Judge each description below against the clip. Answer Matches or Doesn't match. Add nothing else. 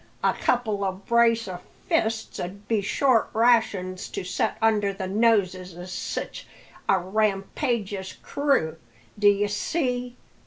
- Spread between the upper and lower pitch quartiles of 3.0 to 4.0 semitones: Matches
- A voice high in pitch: Matches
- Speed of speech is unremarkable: Doesn't match